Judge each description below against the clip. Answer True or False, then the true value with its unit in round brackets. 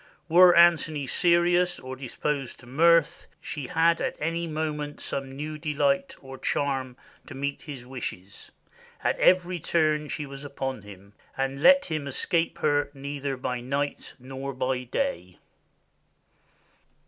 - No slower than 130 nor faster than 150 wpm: True (135 wpm)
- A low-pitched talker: False (145 Hz)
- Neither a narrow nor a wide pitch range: True (3.8 semitones)